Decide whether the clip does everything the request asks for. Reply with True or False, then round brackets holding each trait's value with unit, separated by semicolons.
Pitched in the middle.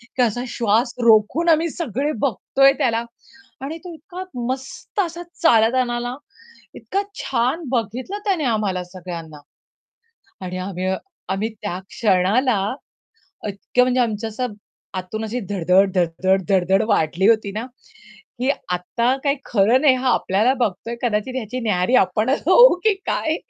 False (230 Hz)